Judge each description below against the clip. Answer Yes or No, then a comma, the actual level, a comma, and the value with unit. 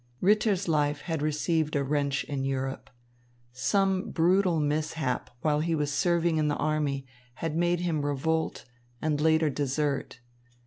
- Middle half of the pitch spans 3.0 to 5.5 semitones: No, narrow, 2.4 semitones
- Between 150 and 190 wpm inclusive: No, average, 140 wpm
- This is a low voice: No, medium, 155 Hz